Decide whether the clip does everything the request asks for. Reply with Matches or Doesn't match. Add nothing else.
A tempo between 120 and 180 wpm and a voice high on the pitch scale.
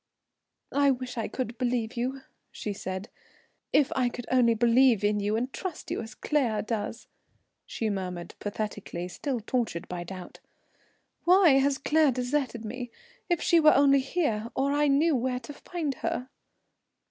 Matches